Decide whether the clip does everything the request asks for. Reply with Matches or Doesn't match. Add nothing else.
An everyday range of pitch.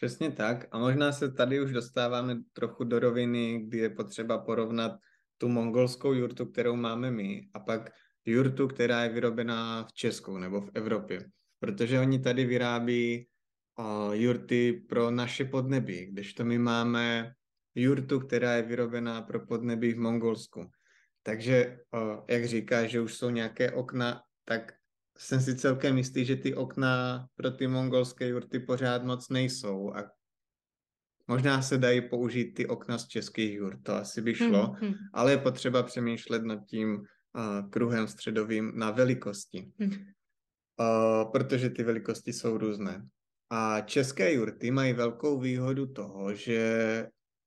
Doesn't match